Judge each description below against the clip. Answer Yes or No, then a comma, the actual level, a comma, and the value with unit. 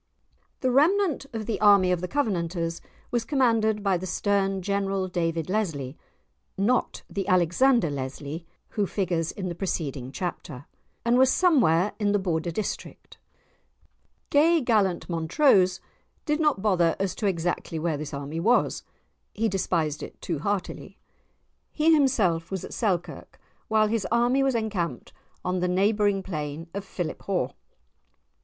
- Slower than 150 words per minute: Yes, average, 140 wpm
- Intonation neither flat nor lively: Yes, average, 4.9 semitones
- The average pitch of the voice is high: Yes, high, 195 Hz